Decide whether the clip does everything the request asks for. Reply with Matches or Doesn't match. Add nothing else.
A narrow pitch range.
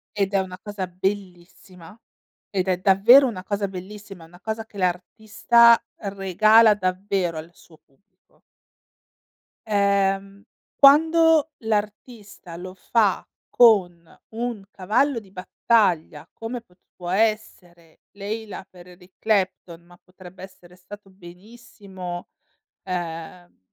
Doesn't match